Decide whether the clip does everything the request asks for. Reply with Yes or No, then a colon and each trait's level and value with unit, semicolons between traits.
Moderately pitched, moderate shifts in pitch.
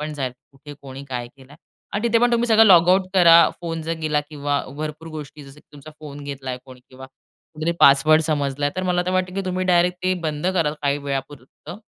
Yes: medium, 155 Hz; average, 4.0 semitones